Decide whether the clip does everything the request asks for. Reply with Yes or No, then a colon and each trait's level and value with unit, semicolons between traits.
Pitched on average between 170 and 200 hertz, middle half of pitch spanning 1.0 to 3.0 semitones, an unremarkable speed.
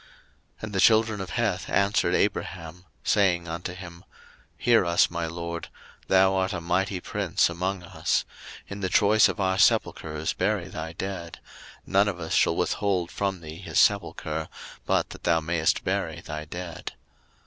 No: very low, 90 Hz; narrow, 2.6 semitones; average, 165 wpm